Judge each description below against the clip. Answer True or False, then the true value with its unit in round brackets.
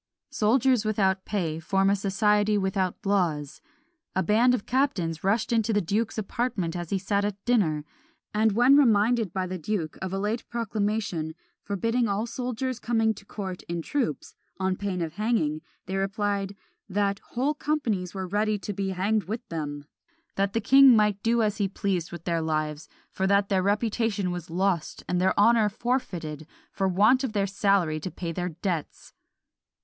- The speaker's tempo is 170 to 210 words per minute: True (175 wpm)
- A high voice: True (200 Hz)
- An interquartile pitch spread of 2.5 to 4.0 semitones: True (3.4 semitones)